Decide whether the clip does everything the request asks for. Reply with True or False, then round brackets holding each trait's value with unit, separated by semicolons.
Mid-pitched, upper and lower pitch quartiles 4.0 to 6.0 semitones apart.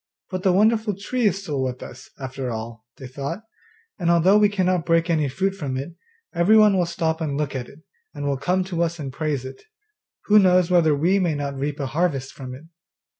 True (165 Hz; 5.1 semitones)